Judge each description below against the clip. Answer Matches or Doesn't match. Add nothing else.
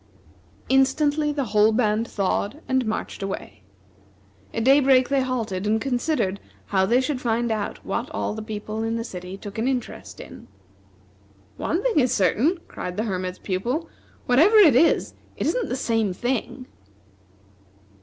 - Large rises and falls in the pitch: Doesn't match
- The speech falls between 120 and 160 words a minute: Matches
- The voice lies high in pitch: Matches